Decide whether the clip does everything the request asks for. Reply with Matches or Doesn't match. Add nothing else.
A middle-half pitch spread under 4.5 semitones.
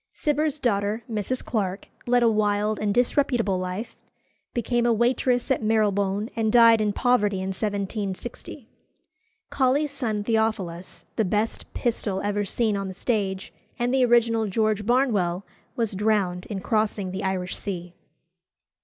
Matches